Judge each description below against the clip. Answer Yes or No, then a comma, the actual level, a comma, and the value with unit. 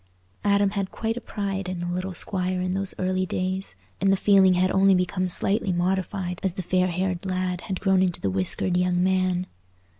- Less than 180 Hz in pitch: No, medium, 185 Hz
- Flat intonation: Yes, narrow, 1.1 semitones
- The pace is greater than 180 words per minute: Yes, average, 200 wpm